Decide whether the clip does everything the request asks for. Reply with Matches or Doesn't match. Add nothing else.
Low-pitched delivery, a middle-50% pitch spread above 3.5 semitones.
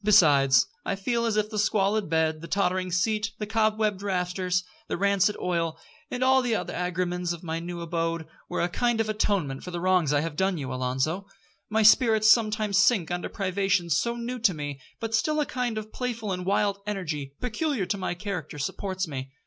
Doesn't match